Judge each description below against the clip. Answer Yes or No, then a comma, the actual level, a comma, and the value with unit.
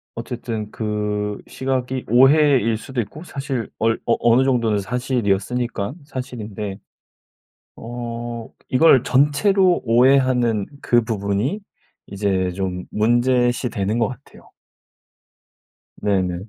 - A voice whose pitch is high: No, low, 120 Hz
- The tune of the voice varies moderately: Yes, average, 3.7 semitones